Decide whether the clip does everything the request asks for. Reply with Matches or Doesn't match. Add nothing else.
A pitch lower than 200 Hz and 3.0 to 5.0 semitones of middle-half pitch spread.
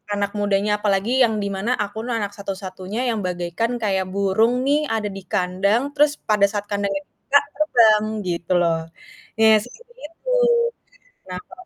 Doesn't match